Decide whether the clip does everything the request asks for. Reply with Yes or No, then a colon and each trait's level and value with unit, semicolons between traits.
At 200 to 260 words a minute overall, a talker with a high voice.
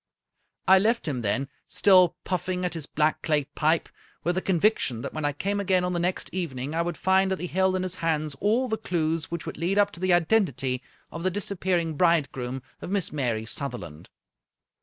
No: fast, 205 wpm; medium, 170 Hz